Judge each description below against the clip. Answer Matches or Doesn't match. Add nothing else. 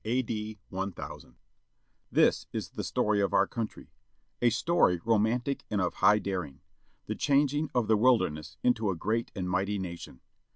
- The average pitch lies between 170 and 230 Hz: Doesn't match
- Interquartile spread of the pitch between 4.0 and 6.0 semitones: Matches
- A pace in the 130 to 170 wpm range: Matches